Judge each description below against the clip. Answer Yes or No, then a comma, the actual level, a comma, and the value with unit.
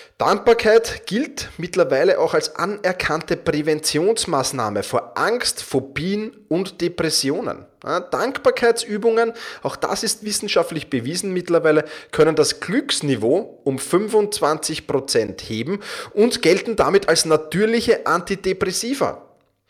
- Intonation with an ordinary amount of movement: No, wide, 6.3 semitones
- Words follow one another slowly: Yes, slow, 95 wpm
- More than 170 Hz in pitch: Yes, high, 190 Hz